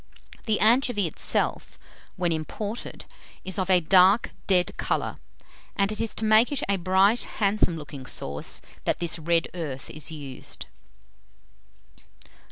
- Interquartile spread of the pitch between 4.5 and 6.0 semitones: Yes, average, 4.8 semitones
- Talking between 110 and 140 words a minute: Yes, slow, 135 wpm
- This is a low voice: No, medium, 185 Hz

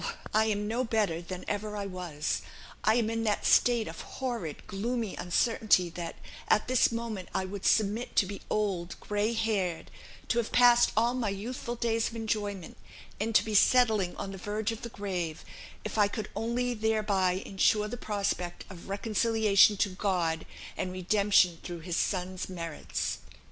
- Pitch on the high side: Yes, high, 210 Hz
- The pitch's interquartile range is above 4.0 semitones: No, average, 3.3 semitones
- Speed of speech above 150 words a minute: Yes, average, 170 wpm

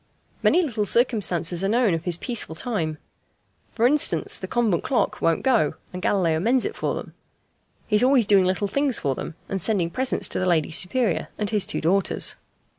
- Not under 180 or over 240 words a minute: Yes, average, 190 wpm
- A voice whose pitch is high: Yes, high, 200 Hz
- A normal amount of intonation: No, wide, 5.8 semitones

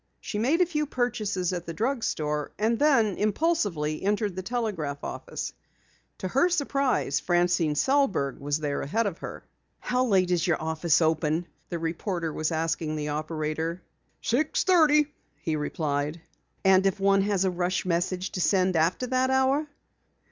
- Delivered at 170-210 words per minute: No, average, 160 wpm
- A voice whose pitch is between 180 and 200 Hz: Yes, medium, 185 Hz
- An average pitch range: No, wide, 6.9 semitones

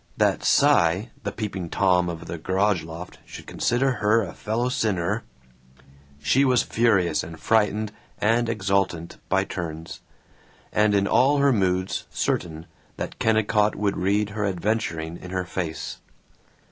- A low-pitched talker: Yes, low, 100 Hz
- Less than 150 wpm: Yes, average, 140 wpm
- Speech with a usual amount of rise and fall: Yes, average, 3.9 semitones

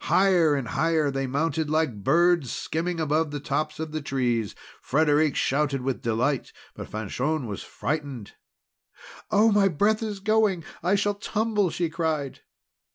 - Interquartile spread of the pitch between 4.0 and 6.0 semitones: Yes, average, 4.6 semitones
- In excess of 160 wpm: No, average, 150 wpm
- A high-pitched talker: No, medium, 155 Hz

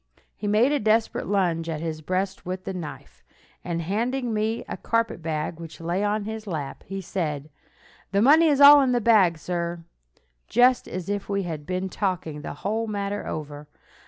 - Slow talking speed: No, average, 180 wpm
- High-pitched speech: Yes, high, 195 Hz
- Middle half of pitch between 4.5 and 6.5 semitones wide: Yes, average, 4.8 semitones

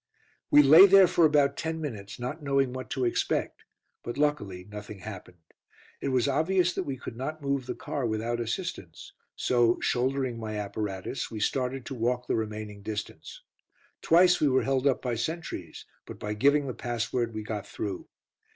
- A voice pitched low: Yes, low, 125 Hz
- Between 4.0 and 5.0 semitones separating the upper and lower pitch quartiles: Yes, average, 4.6 semitones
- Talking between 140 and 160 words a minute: No, average, 175 wpm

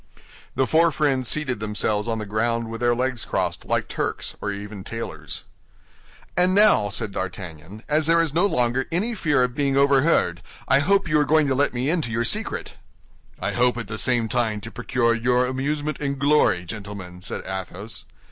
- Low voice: Yes, low, 120 Hz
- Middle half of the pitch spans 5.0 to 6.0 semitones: Yes, wide, 5.5 semitones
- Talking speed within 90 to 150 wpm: No, average, 185 wpm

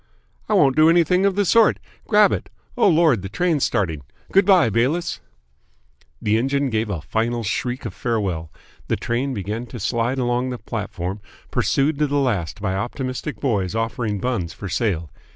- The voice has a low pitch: Yes, low, 120 Hz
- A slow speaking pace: No, average, 170 wpm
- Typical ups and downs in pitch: No, wide, 5.7 semitones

